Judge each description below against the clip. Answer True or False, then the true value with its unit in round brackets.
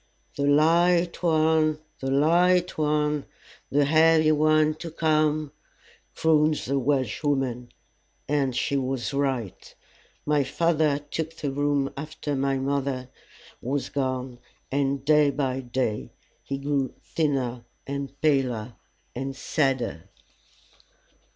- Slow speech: True (110 wpm)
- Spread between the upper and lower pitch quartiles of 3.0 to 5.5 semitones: False (2.6 semitones)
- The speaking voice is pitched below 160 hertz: True (140 Hz)